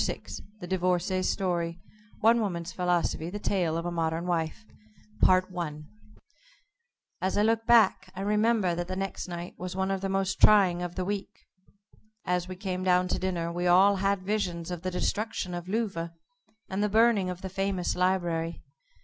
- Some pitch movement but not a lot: No, narrow, 2.1 semitones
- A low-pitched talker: No, medium, 185 Hz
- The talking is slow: No, average, 170 wpm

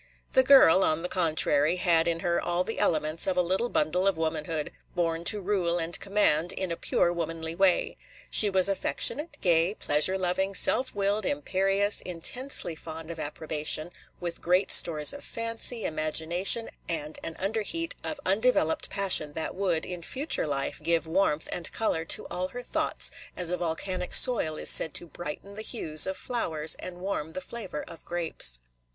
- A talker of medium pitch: Yes, medium, 175 Hz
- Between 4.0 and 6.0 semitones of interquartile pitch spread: No, average, 3.5 semitones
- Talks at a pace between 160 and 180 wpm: Yes, average, 175 wpm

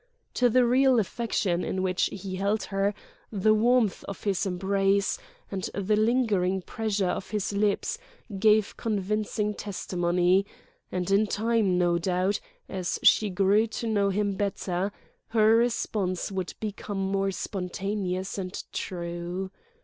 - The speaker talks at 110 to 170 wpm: Yes, slow, 135 wpm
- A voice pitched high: Yes, high, 200 Hz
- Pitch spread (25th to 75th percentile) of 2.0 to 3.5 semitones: Yes, narrow, 2.4 semitones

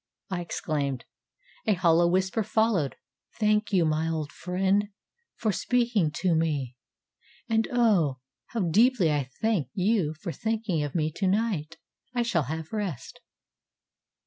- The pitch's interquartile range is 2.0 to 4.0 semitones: No, wide, 5.5 semitones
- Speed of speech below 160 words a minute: Yes, average, 140 wpm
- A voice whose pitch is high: No, medium, 180 Hz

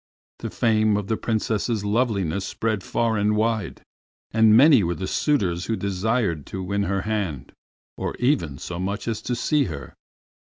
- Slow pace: No, average, 165 wpm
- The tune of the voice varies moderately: Yes, average, 3.2 semitones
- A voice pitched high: No, low, 105 Hz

